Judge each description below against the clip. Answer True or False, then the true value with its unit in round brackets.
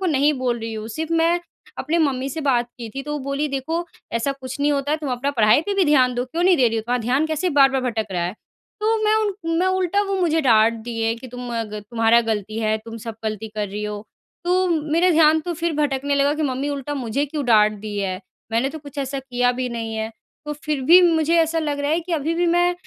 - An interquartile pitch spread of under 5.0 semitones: False (5.5 semitones)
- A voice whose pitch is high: True (275 Hz)